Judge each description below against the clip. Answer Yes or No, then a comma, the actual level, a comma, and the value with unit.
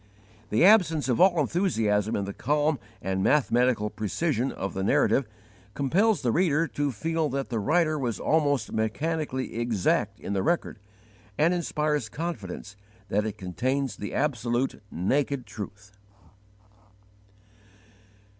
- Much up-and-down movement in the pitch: Yes, wide, 6.4 semitones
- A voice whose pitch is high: No, low, 135 Hz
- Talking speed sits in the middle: No, slow, 125 wpm